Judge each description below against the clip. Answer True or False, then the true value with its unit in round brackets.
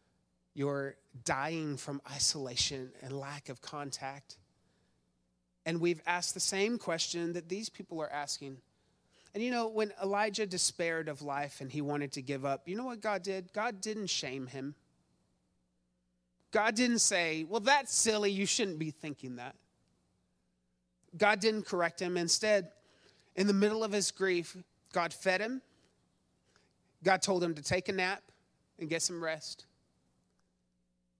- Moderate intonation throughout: False (6.7 semitones)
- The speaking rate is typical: True (150 wpm)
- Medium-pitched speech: True (165 Hz)